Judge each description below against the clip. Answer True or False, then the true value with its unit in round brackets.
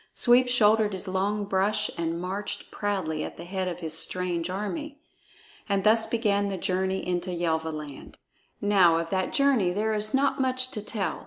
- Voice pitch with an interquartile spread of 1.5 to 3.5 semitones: True (3.2 semitones)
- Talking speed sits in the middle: True (170 wpm)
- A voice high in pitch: True (195 Hz)